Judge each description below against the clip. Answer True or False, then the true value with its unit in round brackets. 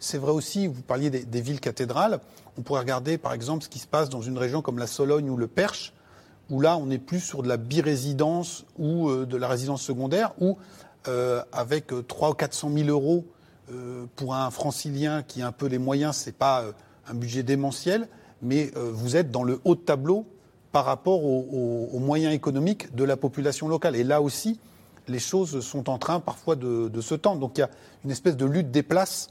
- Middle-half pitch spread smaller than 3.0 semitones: False (3.9 semitones)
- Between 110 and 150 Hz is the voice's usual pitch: True (140 Hz)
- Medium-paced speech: False (230 wpm)